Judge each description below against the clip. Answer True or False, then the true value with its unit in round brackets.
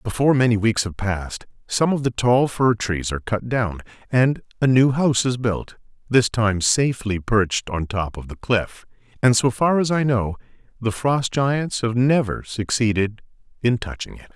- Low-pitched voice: True (115 Hz)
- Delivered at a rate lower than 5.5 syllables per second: True (4.8 syllables/s)